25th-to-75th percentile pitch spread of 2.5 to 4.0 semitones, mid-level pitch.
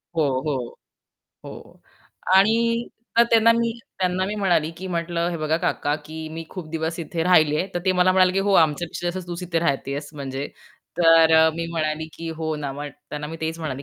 Yes: average, 2.9 semitones; medium, 165 Hz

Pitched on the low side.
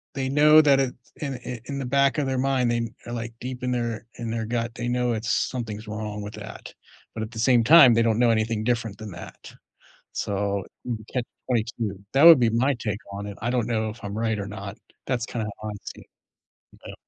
Yes: low, 115 Hz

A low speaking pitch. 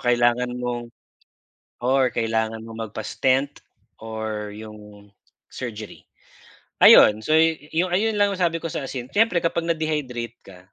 Yes: low, 125 Hz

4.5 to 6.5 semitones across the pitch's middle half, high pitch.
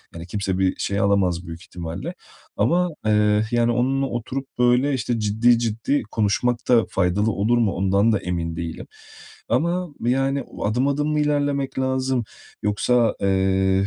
No: average, 5.2 semitones; low, 115 Hz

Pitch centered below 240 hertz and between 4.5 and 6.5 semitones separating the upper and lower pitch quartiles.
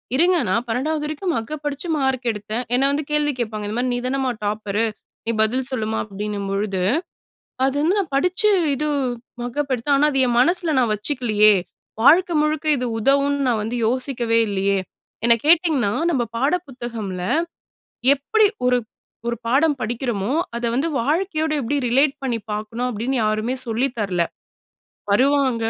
No: very high, 250 Hz; average, 4.8 semitones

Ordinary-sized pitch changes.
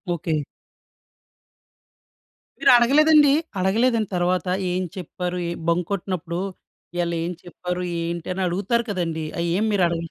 Yes: average, 3.1 semitones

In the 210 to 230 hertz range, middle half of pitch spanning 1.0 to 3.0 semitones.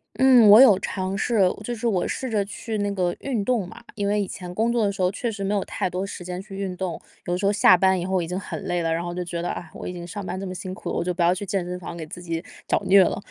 No: high, 190 Hz; narrow, 2.5 semitones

